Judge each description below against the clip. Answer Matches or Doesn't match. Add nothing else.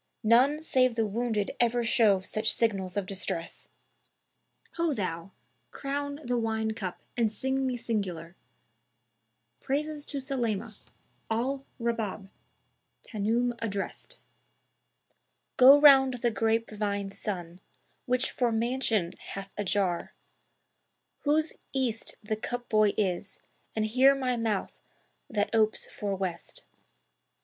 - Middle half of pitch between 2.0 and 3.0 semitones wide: Doesn't match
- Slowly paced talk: Matches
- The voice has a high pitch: Matches